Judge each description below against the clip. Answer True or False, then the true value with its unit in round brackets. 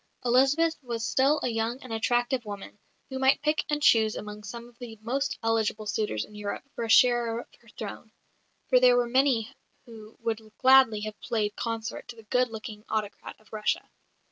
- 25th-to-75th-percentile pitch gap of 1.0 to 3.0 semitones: True (2.6 semitones)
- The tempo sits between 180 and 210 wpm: True (190 wpm)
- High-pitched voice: True (230 Hz)